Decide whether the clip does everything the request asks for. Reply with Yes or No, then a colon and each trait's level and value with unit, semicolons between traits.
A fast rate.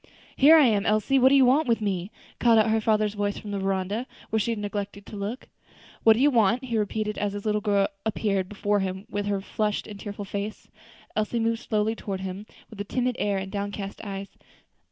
Yes: fast, 220 wpm